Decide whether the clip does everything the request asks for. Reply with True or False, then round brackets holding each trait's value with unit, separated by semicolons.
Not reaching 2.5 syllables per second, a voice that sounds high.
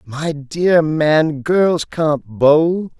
False (2.1 syllables/s; 155 Hz)